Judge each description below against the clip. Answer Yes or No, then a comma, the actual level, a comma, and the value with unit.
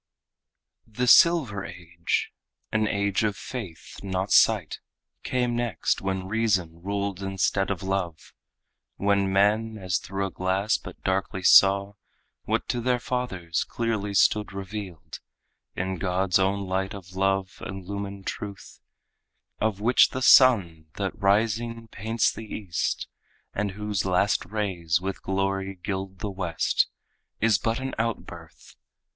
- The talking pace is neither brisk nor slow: No, slow, 130 wpm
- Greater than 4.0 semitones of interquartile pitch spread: No, narrow, 2.4 semitones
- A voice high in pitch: No, low, 100 Hz